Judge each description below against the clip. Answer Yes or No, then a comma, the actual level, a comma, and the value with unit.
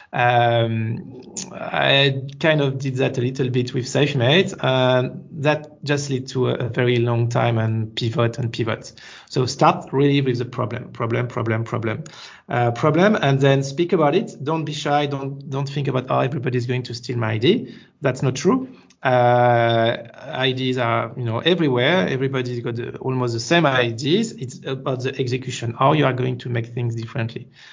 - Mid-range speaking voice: No, low, 130 Hz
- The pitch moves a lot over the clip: No, average, 2.8 semitones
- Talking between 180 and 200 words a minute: Yes, average, 185 wpm